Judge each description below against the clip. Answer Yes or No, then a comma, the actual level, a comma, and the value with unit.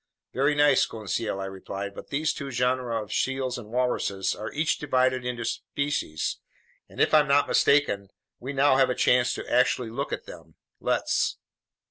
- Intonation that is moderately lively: Yes, average, 3.7 semitones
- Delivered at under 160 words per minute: No, average, 170 wpm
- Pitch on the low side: Yes, low, 125 Hz